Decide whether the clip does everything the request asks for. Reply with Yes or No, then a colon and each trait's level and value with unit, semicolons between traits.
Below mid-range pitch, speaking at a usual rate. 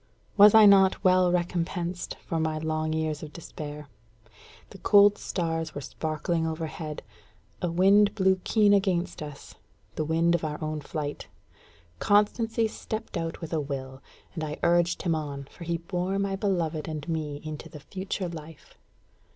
No: medium, 165 Hz; average, 160 wpm